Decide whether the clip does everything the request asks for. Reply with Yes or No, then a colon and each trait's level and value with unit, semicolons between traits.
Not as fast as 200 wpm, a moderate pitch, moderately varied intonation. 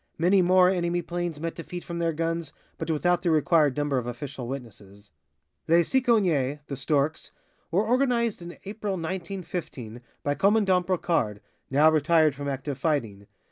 Yes: average, 150 wpm; medium, 165 Hz; average, 4.3 semitones